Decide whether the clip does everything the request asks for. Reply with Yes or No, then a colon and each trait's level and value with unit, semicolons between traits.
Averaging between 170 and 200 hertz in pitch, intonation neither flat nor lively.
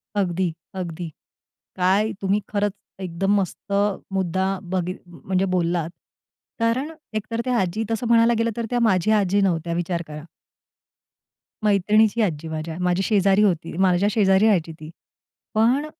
Yes: high, 190 Hz; average, 3.7 semitones